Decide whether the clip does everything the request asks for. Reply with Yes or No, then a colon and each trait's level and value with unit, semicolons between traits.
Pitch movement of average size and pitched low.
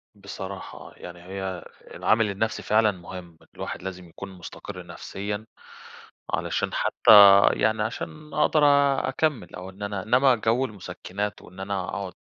Yes: average, 3.0 semitones; low, 100 Hz